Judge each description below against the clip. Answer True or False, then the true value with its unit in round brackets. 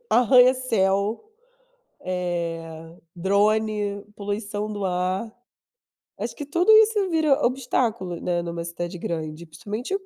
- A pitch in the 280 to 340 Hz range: False (205 Hz)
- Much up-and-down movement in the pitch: True (6.0 semitones)